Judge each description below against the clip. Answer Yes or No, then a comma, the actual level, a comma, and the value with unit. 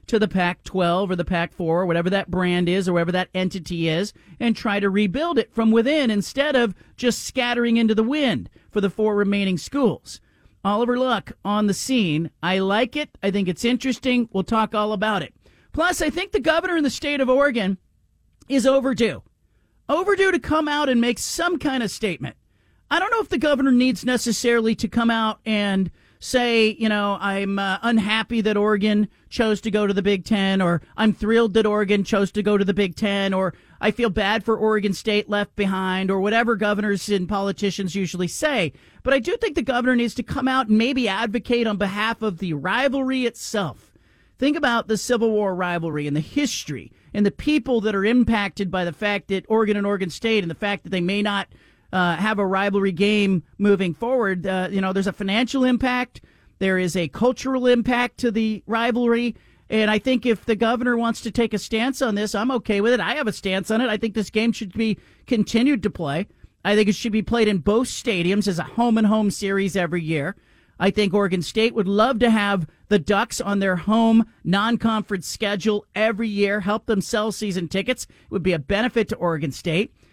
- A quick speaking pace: Yes, fast, 210 wpm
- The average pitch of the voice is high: Yes, high, 215 Hz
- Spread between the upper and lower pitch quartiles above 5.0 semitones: No, average, 3.3 semitones